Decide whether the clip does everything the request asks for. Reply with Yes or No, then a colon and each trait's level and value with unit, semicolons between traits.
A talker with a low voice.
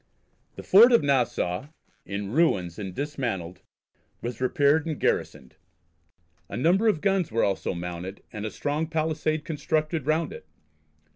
No: medium, 145 Hz